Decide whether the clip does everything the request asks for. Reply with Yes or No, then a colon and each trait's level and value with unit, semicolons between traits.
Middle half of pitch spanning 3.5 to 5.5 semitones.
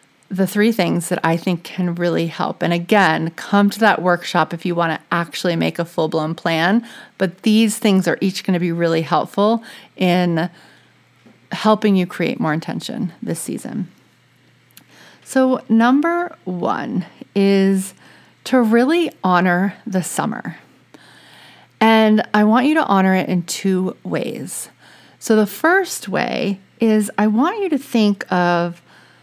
Yes: average, 4.4 semitones